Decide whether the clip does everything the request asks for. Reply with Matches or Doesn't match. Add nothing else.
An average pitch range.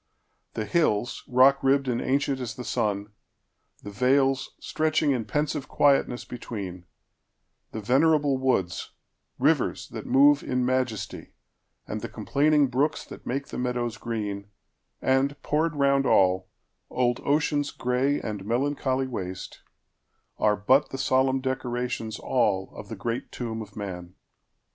Matches